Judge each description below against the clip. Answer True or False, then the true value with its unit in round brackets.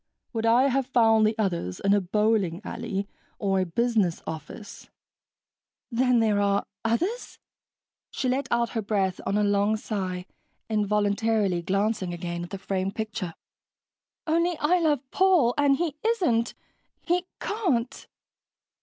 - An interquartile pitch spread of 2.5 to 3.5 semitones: False (4.3 semitones)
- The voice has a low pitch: False (220 Hz)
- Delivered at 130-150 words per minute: True (135 wpm)